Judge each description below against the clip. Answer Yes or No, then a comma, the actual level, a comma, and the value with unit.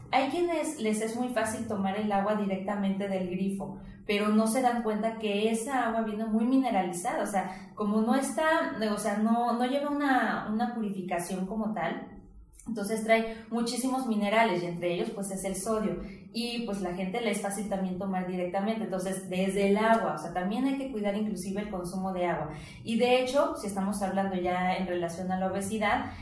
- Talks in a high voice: Yes, high, 210 Hz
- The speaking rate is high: Yes, fast, 195 wpm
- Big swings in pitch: No, average, 3.1 semitones